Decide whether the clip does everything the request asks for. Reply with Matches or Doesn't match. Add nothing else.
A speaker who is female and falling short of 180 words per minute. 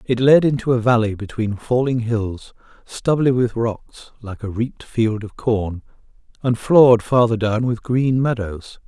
Doesn't match